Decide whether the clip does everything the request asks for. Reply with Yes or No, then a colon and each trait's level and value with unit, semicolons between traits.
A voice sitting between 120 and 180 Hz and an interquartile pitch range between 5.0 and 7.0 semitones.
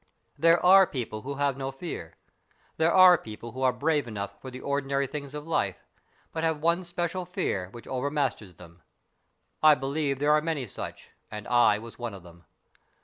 Yes: medium, 140 Hz; wide, 5.6 semitones